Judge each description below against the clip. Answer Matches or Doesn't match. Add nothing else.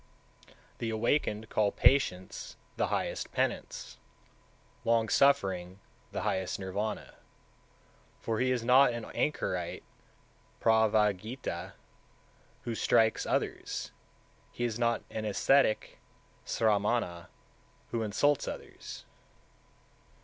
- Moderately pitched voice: Doesn't match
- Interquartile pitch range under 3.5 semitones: Matches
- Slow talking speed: Matches